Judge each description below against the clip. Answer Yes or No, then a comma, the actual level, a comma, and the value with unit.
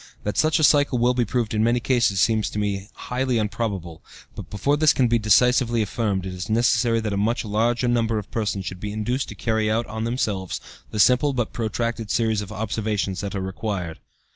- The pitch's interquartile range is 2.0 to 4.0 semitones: Yes, average, 2.7 semitones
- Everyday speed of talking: No, fast, 210 wpm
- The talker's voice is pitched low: Yes, low, 110 Hz